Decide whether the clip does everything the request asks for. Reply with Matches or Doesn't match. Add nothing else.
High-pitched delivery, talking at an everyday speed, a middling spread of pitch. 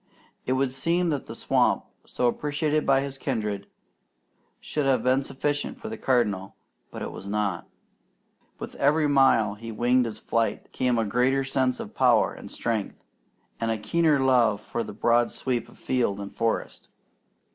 Doesn't match